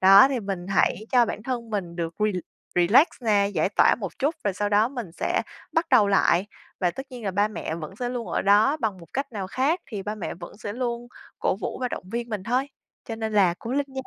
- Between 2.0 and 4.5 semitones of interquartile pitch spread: Yes, average, 4.0 semitones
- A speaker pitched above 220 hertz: No, high, 215 Hz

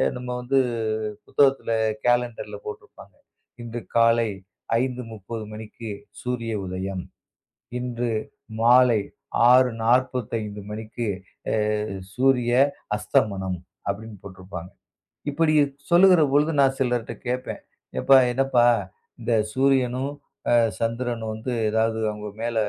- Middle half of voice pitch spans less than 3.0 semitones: Yes, narrow, 2.5 semitones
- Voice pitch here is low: Yes, low, 120 Hz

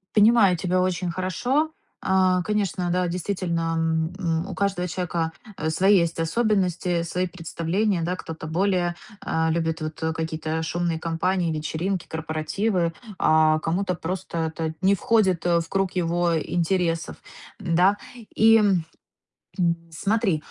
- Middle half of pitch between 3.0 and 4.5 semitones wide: No, narrow, 2.5 semitones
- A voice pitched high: No, medium, 175 Hz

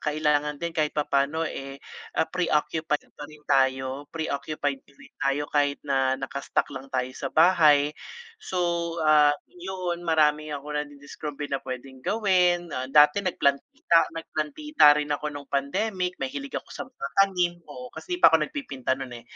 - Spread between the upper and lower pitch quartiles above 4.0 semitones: No, average, 3.7 semitones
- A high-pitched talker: No, medium, 150 Hz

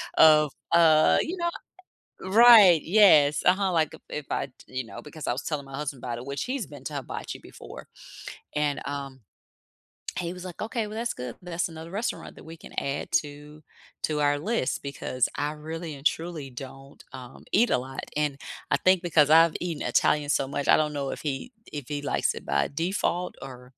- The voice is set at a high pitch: No, medium, 150 Hz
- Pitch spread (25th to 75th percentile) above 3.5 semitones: Yes, average, 4.0 semitones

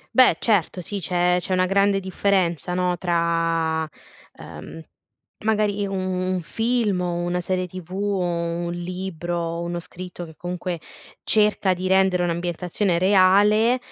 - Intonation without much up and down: Yes, narrow, 2.1 semitones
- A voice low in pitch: No, medium, 180 Hz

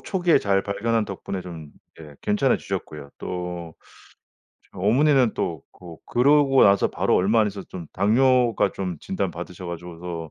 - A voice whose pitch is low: Yes, very low, 95 Hz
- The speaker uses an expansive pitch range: No, average, 5.0 semitones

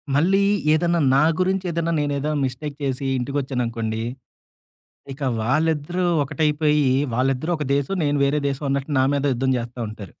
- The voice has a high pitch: No, medium, 145 Hz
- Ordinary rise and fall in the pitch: Yes, average, 3.1 semitones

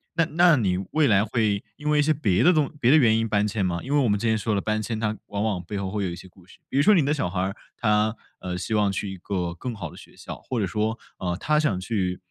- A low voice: Yes, low, 105 Hz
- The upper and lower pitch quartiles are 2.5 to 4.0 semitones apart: No, average, 5.1 semitones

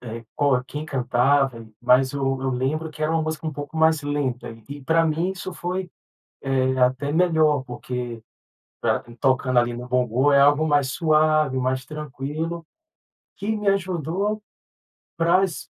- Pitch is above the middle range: No, medium, 145 Hz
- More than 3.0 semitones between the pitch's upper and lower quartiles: Yes, average, 3.6 semitones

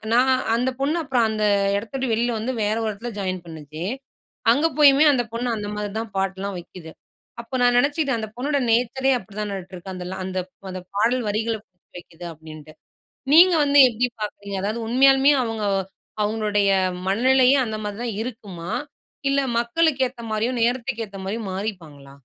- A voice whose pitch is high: Yes, high, 220 Hz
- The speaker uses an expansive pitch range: No, average, 4.3 semitones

